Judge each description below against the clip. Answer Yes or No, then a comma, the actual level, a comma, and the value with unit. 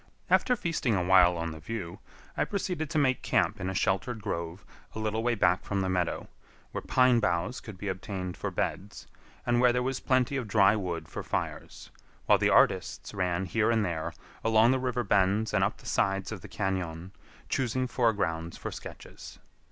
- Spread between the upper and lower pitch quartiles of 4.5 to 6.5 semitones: Yes, average, 4.8 semitones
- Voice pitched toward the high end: No, low, 100 Hz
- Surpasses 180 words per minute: Yes, average, 190 wpm